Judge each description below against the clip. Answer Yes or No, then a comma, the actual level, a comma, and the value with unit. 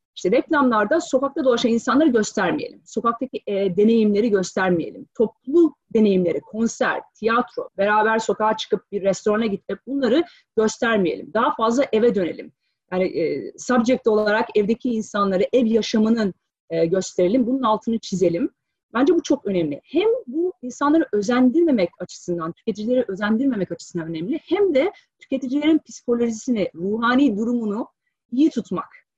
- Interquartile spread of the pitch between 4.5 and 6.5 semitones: Yes, average, 4.9 semitones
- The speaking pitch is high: Yes, high, 230 Hz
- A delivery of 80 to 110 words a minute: No, average, 125 wpm